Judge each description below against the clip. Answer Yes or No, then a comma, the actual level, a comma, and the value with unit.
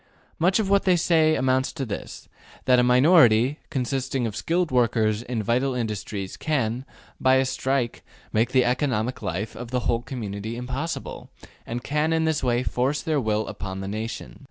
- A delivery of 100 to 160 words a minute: No, average, 175 wpm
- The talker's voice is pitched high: No, low, 125 Hz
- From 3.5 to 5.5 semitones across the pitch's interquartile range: Yes, average, 4.0 semitones